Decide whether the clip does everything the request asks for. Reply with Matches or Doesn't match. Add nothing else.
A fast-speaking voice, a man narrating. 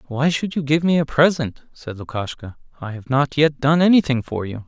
Matches